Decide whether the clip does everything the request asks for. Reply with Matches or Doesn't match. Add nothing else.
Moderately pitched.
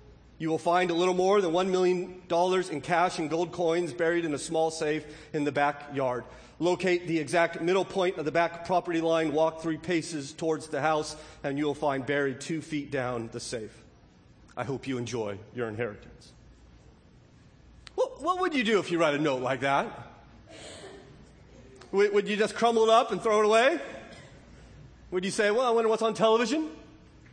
Matches